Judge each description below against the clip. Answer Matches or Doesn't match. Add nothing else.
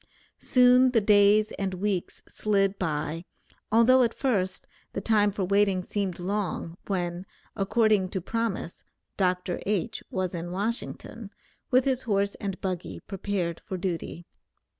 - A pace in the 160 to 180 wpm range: Doesn't match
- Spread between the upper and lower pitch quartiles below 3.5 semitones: Matches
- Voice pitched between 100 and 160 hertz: Doesn't match